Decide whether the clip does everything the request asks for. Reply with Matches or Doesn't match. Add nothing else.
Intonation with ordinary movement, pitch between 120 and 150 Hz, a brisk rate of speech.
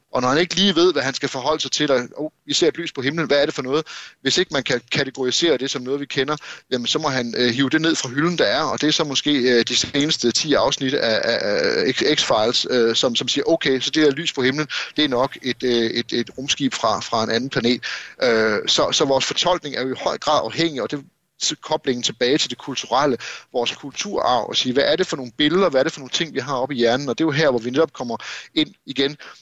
Matches